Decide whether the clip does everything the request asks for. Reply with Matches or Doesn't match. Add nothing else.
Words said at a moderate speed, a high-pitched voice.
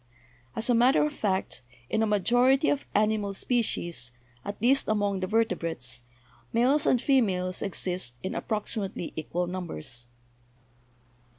Doesn't match